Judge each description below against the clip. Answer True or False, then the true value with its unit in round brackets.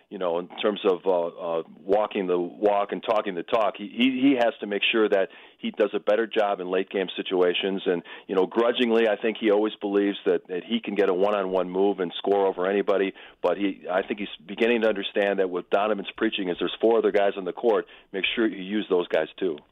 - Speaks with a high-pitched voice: False (100 Hz)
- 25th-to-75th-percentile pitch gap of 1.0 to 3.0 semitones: True (2.7 semitones)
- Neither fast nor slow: False (235 wpm)